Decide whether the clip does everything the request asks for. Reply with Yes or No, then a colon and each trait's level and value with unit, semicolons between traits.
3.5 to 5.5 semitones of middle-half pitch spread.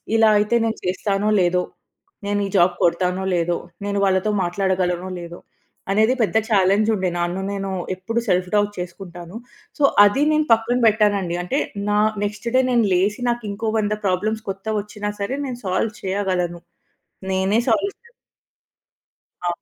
No: average, 3.0 semitones